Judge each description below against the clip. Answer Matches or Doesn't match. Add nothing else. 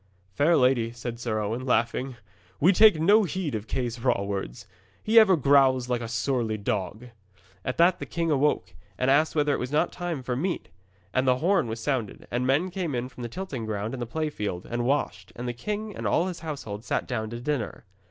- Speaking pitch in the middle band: Doesn't match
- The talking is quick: Matches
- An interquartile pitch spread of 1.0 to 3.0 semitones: Doesn't match